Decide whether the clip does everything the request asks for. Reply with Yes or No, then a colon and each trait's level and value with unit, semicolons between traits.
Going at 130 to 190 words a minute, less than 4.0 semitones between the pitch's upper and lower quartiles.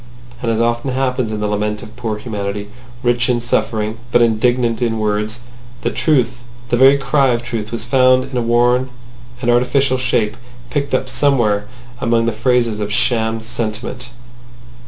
Yes: average, 155 wpm; narrow, 2.4 semitones